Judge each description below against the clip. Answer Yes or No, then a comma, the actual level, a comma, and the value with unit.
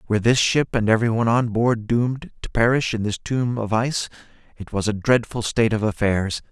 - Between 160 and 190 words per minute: No, fast, 205 wpm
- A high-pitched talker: No, low, 115 Hz